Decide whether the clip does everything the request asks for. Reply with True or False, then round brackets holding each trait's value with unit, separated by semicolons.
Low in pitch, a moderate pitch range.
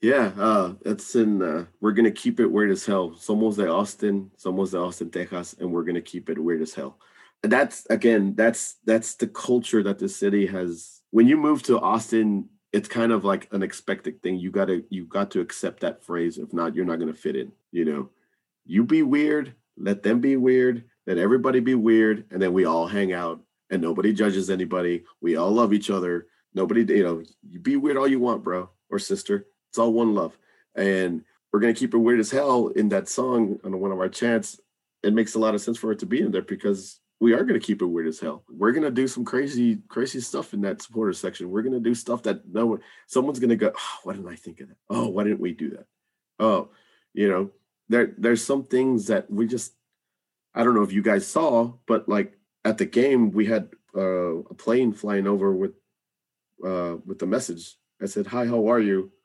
True (110 Hz; 4.1 semitones)